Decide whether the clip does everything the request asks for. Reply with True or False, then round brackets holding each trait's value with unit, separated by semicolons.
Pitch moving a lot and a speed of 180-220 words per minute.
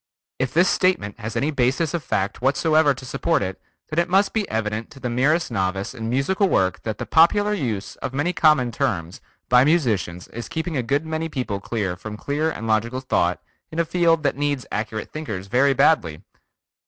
True (6.7 semitones; 190 wpm)